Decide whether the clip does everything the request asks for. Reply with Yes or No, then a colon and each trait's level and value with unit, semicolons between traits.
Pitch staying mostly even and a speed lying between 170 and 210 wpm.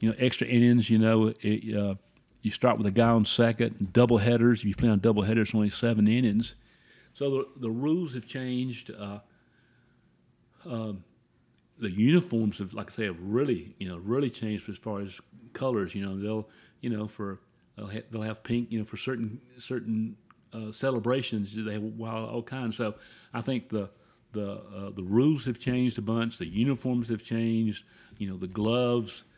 Yes: narrow, 2.3 semitones; average, 190 wpm